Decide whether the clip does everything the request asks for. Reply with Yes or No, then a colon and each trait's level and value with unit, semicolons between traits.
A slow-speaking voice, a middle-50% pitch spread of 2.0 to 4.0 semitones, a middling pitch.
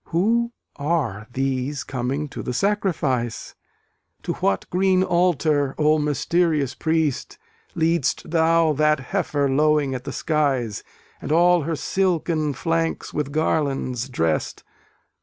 Yes: slow, 120 wpm; average, 3.7 semitones; medium, 150 Hz